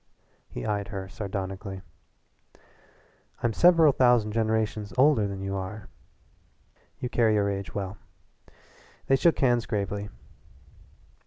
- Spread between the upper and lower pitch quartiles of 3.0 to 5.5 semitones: Yes, average, 3.4 semitones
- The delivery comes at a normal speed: No, slow, 110 wpm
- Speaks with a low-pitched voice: Yes, low, 105 Hz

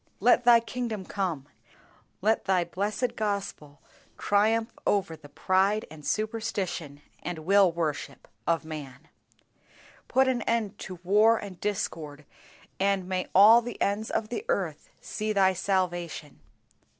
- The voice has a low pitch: No, high, 195 Hz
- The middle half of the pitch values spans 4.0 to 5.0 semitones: Yes, average, 4.4 semitones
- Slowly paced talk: Yes, slow, 130 wpm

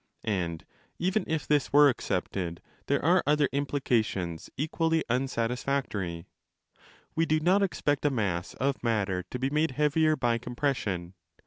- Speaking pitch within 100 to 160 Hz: Yes, low, 135 Hz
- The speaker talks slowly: Yes, slow, 130 wpm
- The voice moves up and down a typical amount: No, wide, 6.7 semitones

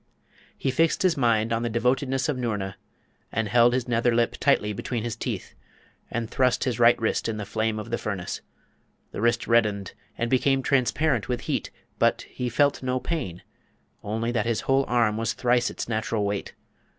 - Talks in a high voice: No, low, 120 Hz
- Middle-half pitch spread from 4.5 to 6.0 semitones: No, narrow, 2.5 semitones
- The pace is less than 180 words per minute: No, average, 185 wpm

